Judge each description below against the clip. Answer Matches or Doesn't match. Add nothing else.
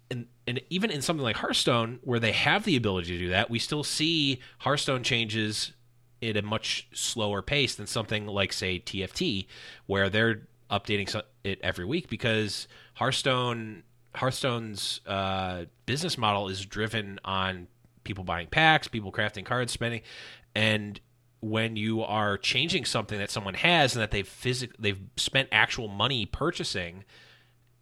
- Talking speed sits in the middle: Matches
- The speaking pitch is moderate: Doesn't match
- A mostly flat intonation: Doesn't match